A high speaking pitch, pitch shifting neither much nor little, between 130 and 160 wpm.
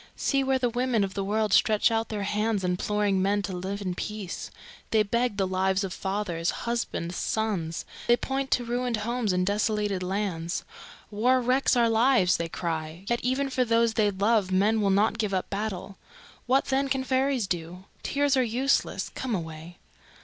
No: high, 210 Hz; average, 4.1 semitones; average, 180 wpm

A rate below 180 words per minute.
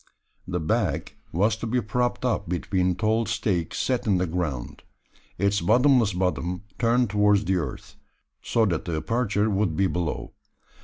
Yes: average, 155 wpm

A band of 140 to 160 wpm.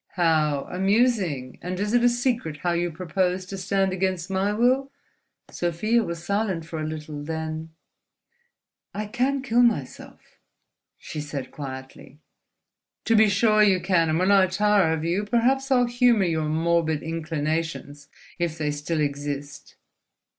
Yes: average, 145 wpm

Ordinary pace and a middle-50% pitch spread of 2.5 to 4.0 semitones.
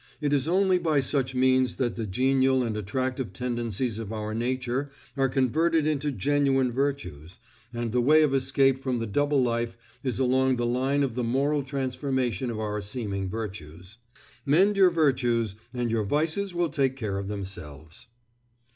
Yes: average, 165 wpm; average, 3.6 semitones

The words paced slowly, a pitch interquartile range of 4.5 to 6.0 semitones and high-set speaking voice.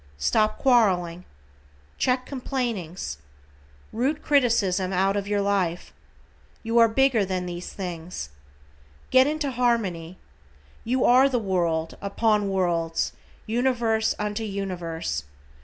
Yes: slow, 110 wpm; average, 5.2 semitones; high, 200 Hz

